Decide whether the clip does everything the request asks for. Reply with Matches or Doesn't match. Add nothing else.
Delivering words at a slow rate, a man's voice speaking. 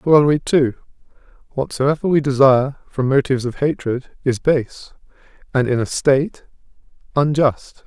Matches